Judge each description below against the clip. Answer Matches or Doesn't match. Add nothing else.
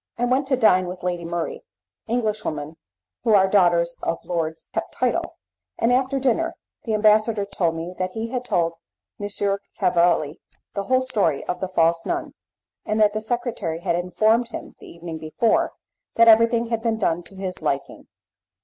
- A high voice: Matches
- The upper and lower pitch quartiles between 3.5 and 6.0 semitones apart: Matches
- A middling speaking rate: Matches